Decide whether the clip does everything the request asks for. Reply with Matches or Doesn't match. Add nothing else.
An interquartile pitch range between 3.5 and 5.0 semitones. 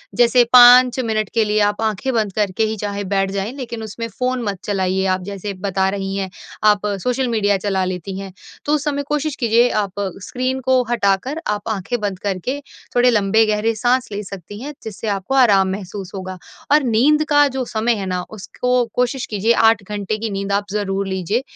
Matches